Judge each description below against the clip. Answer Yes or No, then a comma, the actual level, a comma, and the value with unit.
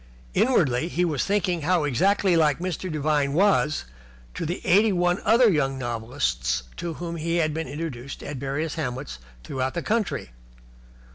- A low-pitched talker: No, medium, 155 Hz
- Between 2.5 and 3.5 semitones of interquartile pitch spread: No, average, 4.7 semitones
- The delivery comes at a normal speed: Yes, average, 155 wpm